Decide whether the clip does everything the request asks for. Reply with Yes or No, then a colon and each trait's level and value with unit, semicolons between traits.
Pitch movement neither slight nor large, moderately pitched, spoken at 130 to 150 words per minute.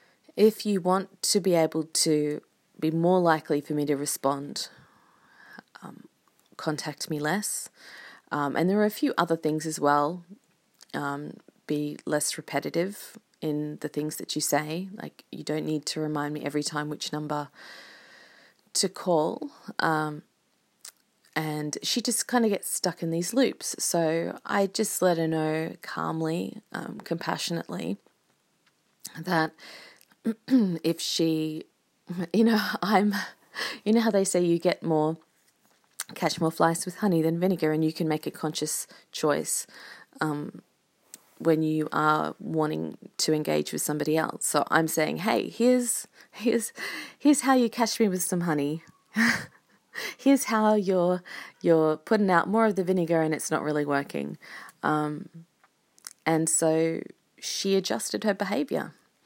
Yes: average, 5.0 semitones; medium, 165 Hz; average, 145 wpm